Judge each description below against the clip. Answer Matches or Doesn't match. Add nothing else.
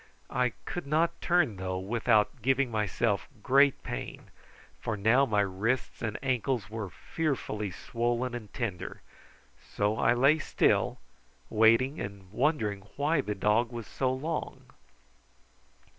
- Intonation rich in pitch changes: Doesn't match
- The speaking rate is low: Matches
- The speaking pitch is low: Matches